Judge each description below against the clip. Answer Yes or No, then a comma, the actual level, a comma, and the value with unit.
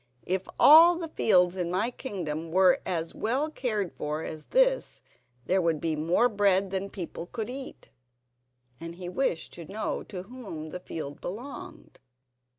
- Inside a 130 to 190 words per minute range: Yes, average, 160 wpm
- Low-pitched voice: No, high, 190 Hz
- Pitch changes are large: Yes, wide, 6.2 semitones